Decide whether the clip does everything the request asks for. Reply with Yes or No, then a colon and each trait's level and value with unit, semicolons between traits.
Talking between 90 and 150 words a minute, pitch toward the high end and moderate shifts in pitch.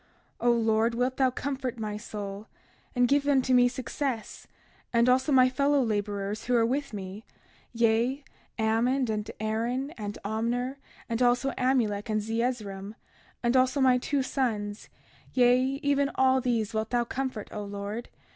Yes: average, 145 wpm; high, 240 Hz; average, 3.0 semitones